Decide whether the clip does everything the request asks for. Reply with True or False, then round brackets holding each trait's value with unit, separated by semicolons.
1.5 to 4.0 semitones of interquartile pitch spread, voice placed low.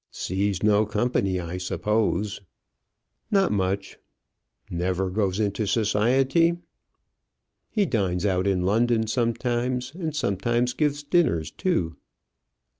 False (4.7 semitones; 105 Hz)